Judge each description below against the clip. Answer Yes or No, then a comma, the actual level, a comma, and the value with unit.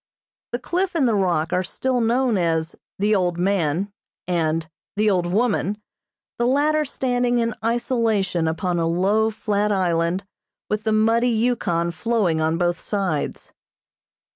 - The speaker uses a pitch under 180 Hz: No, high, 200 Hz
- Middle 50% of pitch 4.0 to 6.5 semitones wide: Yes, average, 5.2 semitones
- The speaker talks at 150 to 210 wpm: No, average, 140 wpm